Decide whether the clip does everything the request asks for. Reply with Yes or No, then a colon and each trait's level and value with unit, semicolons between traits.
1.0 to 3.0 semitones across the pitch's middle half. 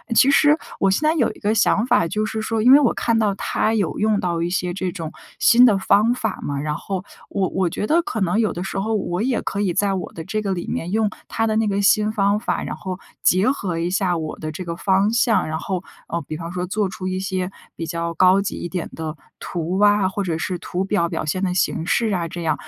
No: average, 3.5 semitones